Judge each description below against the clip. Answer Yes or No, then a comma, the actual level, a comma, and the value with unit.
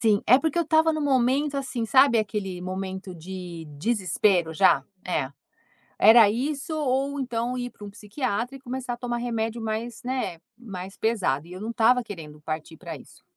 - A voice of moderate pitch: No, high, 225 Hz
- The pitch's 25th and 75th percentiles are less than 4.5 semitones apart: No, average, 5.3 semitones